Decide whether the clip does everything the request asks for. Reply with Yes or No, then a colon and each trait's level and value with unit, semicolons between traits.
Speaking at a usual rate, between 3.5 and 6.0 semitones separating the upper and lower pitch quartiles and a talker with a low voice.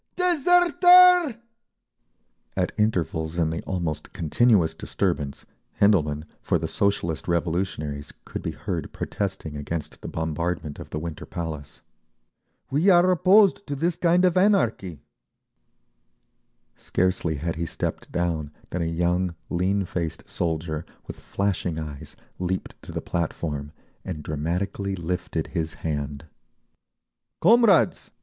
No: slow, 120 wpm; average, 5.2 semitones; very low, 85 Hz